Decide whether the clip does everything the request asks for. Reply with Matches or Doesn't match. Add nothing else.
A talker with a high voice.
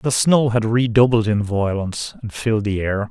Doesn't match